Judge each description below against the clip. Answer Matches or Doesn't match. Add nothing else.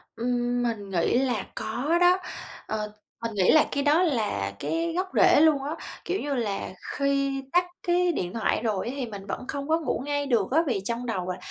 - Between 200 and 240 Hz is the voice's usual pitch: Doesn't match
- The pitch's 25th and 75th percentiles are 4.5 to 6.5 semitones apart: Matches